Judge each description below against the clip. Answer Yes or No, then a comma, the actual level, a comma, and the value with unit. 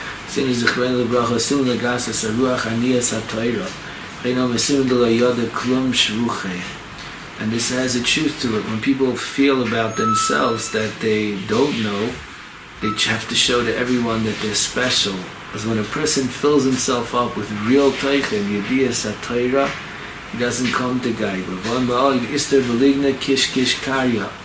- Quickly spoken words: No, average, 185 wpm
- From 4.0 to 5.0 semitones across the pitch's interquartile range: No, average, 2.8 semitones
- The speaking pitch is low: Yes, low, 125 Hz